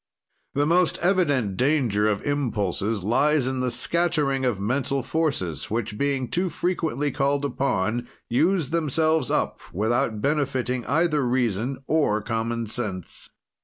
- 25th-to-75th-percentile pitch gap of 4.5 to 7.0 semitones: Yes, average, 4.8 semitones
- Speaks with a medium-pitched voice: No, low, 130 Hz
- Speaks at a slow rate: Yes, slow, 130 wpm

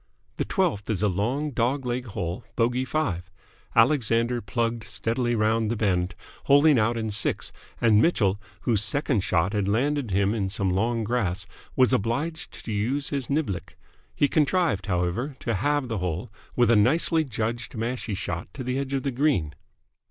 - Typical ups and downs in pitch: Yes, average, 4.7 semitones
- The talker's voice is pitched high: No, low, 115 Hz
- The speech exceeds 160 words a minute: Yes, average, 170 wpm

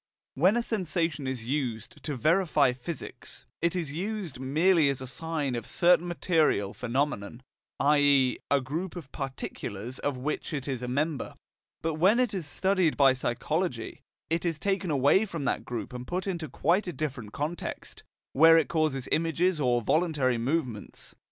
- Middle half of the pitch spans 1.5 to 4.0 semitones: No, average, 4.7 semitones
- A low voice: No, medium, 150 Hz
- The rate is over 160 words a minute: Yes, average, 170 wpm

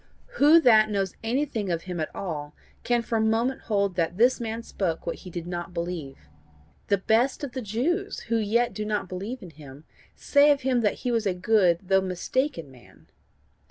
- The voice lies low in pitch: No, high, 210 Hz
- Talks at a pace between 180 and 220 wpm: Yes, average, 195 wpm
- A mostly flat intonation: No, average, 5.2 semitones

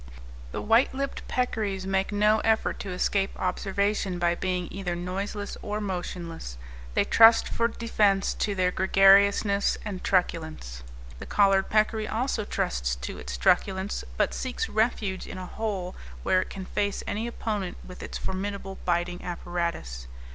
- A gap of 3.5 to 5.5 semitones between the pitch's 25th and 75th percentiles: No, average, 2.8 semitones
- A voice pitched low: No, high, 195 Hz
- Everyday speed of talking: Yes, average, 145 wpm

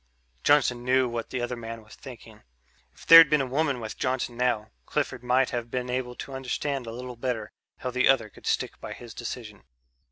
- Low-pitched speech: Yes, low, 125 Hz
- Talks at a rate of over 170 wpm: Yes, average, 200 wpm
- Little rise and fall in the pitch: Yes, narrow, 1.8 semitones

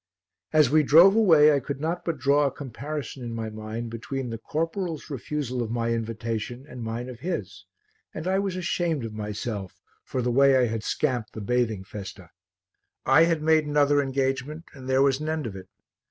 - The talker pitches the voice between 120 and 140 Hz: Yes, low, 135 Hz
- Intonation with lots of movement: No, average, 4.9 semitones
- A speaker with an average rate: Yes, average, 195 wpm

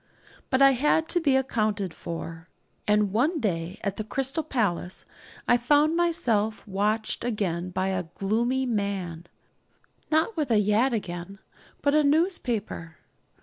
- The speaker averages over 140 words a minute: No, slow, 135 wpm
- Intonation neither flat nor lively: No, wide, 6.0 semitones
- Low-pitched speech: No, high, 215 Hz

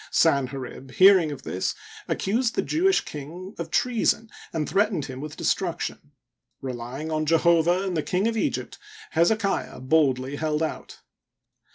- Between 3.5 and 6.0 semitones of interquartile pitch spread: Yes, average, 5.2 semitones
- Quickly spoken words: No, average, 145 wpm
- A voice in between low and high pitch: Yes, medium, 160 Hz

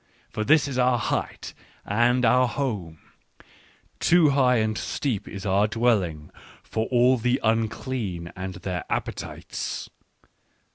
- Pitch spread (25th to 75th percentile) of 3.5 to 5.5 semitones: Yes, average, 4.2 semitones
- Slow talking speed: Yes, slow, 130 wpm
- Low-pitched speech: Yes, low, 115 Hz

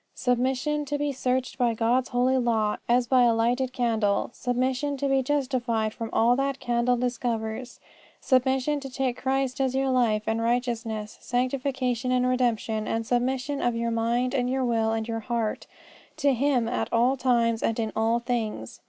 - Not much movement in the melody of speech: Yes, narrow, 2.3 semitones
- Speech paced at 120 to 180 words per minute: Yes, average, 175 wpm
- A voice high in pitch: Yes, high, 245 Hz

